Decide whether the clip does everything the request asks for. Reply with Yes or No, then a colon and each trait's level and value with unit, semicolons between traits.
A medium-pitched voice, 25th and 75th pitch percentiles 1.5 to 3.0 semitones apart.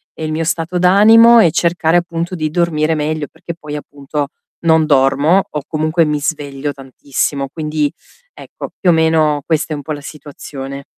Yes: medium, 155 Hz; narrow, 2.4 semitones